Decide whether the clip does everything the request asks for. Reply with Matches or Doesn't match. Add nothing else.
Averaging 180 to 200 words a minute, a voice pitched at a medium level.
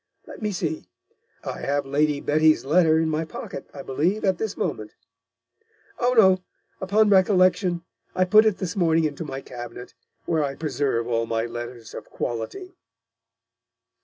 Doesn't match